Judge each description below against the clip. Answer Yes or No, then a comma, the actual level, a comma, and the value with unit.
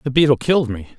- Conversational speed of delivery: No, fast, 245 wpm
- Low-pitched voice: Yes, low, 130 Hz